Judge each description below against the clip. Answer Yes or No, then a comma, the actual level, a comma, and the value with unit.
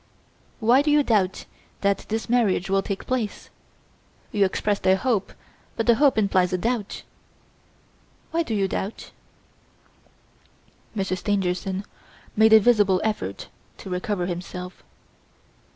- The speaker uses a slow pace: Yes, slow, 125 wpm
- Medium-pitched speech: No, high, 200 Hz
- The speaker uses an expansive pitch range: No, average, 3.2 semitones